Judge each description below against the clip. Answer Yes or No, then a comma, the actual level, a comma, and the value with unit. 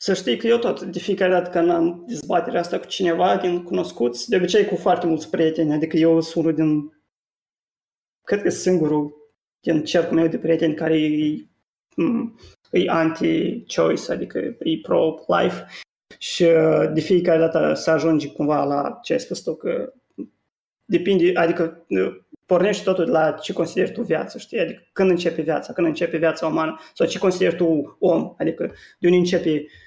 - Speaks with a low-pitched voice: No, medium, 165 Hz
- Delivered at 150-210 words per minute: Yes, average, 165 wpm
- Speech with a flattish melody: Yes, narrow, 2.1 semitones